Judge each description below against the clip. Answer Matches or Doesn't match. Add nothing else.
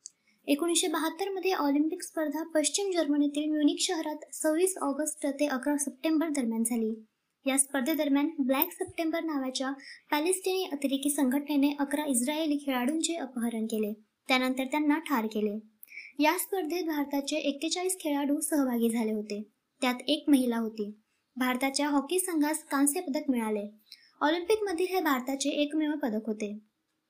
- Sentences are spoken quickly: Doesn't match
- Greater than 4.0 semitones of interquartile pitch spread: Doesn't match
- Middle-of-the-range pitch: Doesn't match